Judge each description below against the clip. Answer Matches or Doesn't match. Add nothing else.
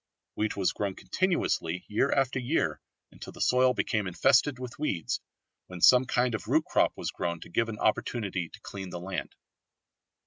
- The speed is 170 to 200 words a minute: Matches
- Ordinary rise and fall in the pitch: Doesn't match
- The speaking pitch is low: Matches